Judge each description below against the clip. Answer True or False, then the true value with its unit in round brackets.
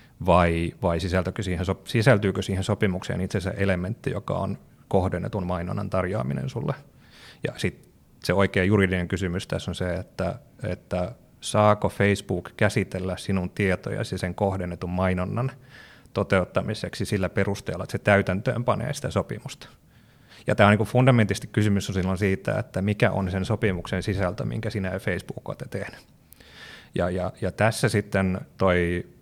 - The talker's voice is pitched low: True (95 Hz)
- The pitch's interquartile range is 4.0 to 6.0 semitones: False (2.5 semitones)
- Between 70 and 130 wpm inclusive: False (140 wpm)